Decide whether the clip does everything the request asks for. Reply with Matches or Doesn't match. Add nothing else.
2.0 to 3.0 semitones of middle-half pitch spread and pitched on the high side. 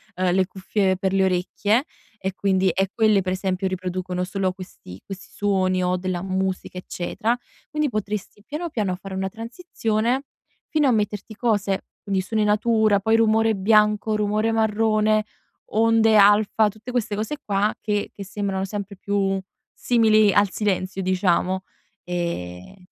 Matches